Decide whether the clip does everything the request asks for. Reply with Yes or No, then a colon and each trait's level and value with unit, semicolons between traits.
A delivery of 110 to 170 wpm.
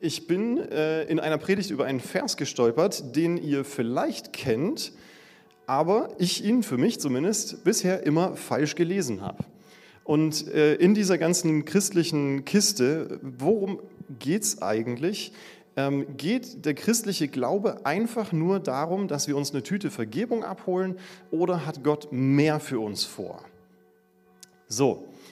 Yes: average, 135 wpm